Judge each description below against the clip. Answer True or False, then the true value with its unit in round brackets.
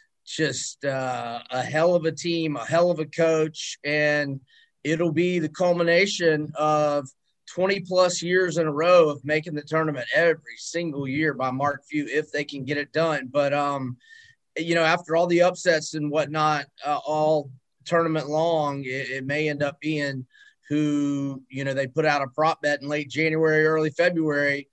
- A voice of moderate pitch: True (155 Hz)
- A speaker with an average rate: True (180 wpm)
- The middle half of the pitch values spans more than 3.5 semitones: False (2.4 semitones)